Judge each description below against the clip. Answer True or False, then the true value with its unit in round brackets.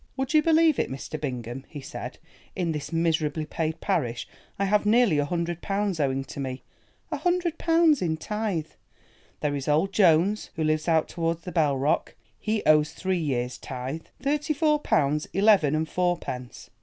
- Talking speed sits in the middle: True (170 wpm)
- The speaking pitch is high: False (165 Hz)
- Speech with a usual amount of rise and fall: False (6.1 semitones)